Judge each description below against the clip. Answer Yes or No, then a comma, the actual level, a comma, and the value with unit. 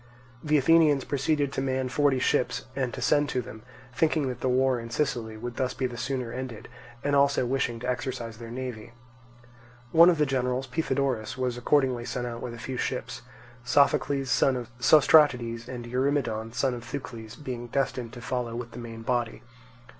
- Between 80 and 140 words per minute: No, average, 180 wpm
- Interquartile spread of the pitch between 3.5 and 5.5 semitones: No, narrow, 2.5 semitones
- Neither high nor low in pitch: No, low, 125 Hz